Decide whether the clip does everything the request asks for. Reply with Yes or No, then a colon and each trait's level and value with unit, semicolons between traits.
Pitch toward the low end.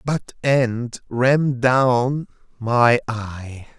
Yes: low, 125 Hz